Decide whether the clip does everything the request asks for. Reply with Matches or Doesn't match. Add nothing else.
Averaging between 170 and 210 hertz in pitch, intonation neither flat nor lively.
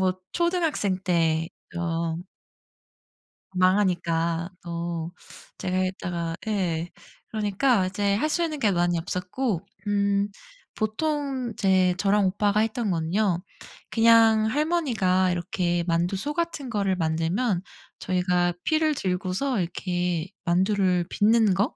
Matches